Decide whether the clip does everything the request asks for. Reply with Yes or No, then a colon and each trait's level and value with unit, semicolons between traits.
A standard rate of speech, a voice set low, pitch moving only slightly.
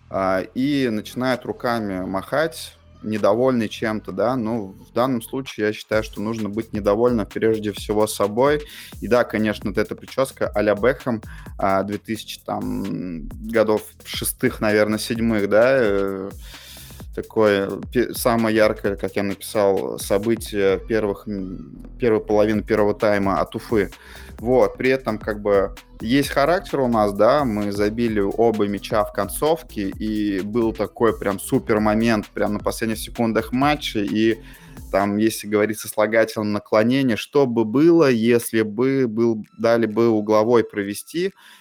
Yes: average, 135 wpm; low, 110 Hz; narrow, 2.3 semitones